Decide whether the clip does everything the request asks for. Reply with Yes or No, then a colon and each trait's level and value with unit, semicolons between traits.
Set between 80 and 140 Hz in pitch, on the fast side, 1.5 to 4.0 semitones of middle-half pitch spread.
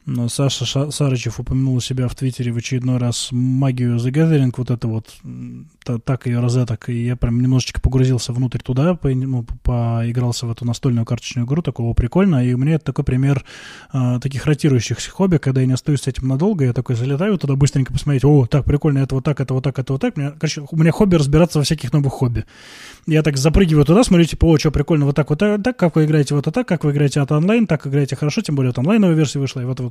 Yes: low, 135 Hz; fast, 245 wpm; average, 3.5 semitones